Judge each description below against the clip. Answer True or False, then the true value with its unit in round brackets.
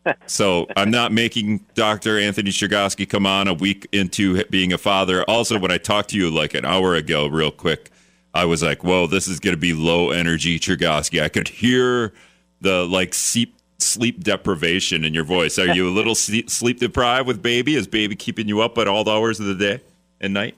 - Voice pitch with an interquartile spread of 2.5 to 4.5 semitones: True (3.9 semitones)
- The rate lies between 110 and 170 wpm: False (205 wpm)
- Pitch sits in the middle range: False (100 Hz)